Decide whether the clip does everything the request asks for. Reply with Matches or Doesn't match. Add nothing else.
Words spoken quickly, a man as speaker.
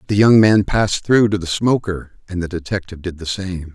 Matches